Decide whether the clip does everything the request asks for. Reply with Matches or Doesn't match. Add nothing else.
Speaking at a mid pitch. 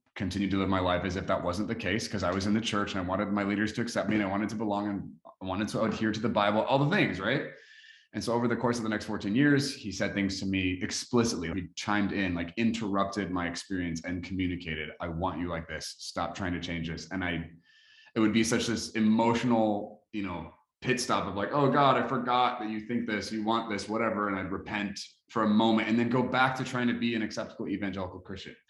Doesn't match